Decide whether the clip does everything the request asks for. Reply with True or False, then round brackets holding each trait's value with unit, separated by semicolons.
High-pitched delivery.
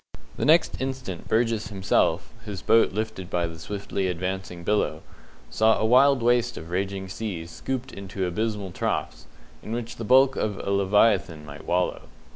False (100 Hz)